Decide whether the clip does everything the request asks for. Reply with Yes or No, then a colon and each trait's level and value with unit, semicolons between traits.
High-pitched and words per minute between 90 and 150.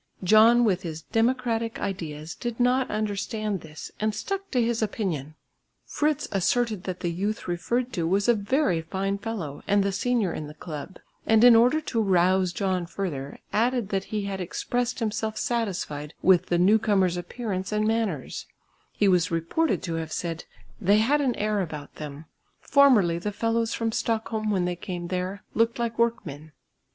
No: high, 205 Hz; average, 170 wpm